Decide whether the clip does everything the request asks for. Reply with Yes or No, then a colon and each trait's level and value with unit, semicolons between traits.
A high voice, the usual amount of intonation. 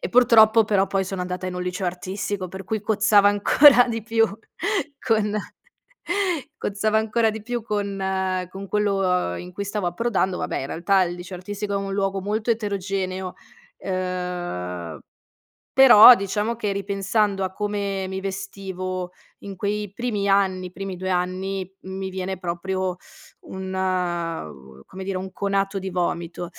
No: high, 195 Hz; narrow, 2.1 semitones